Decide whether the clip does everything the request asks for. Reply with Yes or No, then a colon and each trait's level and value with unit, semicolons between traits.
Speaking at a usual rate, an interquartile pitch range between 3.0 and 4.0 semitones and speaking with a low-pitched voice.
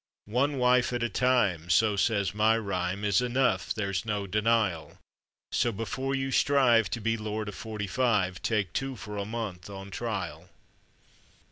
Yes: average, 160 wpm; average, 3.4 semitones; low, 110 Hz